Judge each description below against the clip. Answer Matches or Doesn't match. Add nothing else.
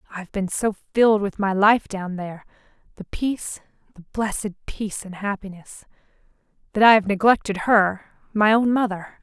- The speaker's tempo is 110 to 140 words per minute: Matches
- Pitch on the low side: Doesn't match